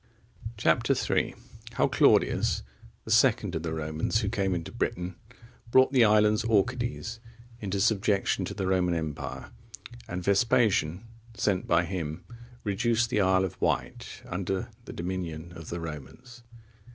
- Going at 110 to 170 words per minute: Yes, average, 140 wpm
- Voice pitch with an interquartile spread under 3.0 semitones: No, average, 4.6 semitones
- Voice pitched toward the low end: Yes, very low, 95 Hz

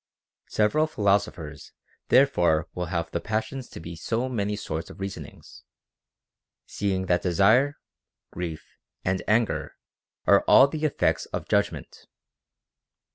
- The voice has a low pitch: Yes, low, 100 Hz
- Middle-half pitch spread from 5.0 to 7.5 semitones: Yes, average, 5.3 semitones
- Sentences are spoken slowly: Yes, slow, 120 wpm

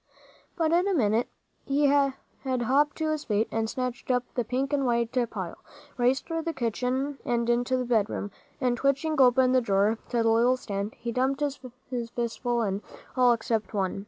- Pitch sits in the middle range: No, very high, 250 Hz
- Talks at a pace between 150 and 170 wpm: No, average, 185 wpm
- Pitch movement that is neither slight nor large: Yes, average, 3.0 semitones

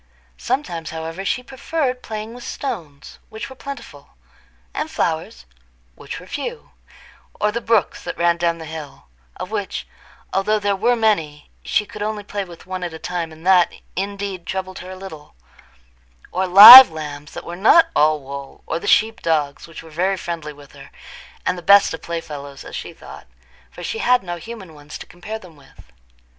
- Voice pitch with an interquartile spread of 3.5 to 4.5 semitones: No, average, 5.3 semitones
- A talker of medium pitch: Yes, medium, 175 Hz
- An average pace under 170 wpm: No, average, 180 wpm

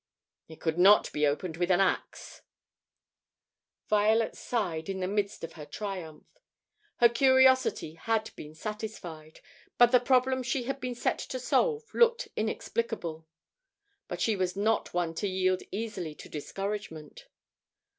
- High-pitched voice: Yes, high, 205 Hz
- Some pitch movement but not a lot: No, wide, 5.7 semitones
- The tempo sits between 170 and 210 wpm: No, average, 140 wpm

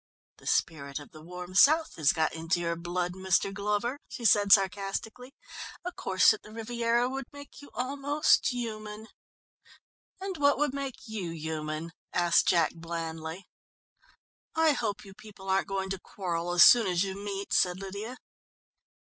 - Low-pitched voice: No, high, 195 Hz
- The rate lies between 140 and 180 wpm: Yes, average, 155 wpm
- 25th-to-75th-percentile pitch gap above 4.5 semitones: Yes, wide, 5.5 semitones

